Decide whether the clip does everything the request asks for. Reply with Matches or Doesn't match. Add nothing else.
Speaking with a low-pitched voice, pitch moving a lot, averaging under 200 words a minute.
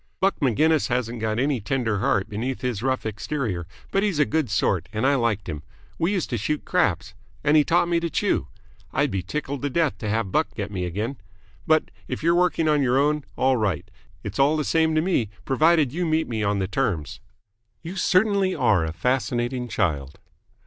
Doesn't match